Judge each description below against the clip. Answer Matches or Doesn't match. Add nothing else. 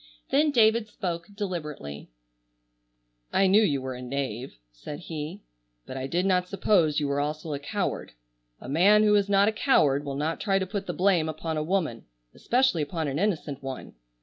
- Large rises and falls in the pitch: Matches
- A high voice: Doesn't match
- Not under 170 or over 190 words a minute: Matches